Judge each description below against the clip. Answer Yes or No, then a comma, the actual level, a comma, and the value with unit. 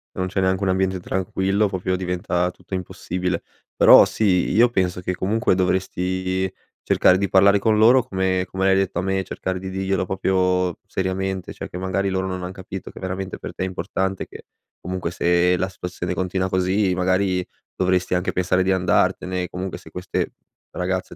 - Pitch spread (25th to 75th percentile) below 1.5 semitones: Yes, narrow, 0.9 semitones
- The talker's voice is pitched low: Yes, very low, 95 Hz